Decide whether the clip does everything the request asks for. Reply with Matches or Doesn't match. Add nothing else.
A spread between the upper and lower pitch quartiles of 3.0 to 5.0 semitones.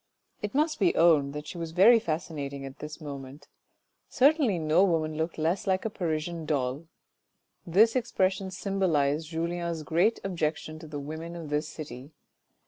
Matches